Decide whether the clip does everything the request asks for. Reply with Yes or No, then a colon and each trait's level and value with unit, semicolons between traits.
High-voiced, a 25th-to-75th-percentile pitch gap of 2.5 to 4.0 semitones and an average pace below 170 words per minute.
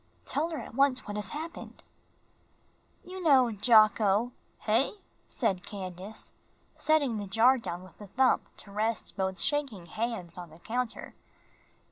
No: high, 220 Hz; average, 5.1 semitones; average, 145 wpm